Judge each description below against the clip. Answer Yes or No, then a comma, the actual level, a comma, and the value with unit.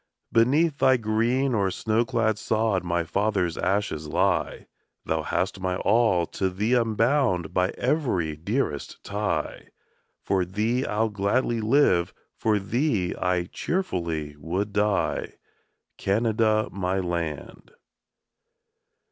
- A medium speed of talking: No, slow, 115 wpm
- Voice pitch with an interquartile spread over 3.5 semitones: Yes, average, 4.2 semitones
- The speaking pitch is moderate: No, low, 105 Hz